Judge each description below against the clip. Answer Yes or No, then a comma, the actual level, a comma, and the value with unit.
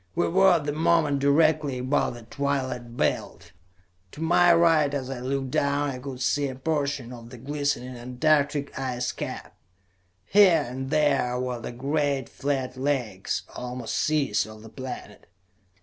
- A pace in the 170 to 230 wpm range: No, average, 155 wpm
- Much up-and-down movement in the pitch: No, average, 2.8 semitones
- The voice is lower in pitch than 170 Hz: Yes, medium, 140 Hz